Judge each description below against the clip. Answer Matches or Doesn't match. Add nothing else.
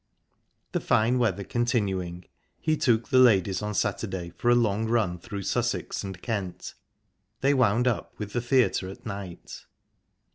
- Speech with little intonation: Doesn't match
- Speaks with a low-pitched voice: Matches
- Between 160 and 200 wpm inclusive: Doesn't match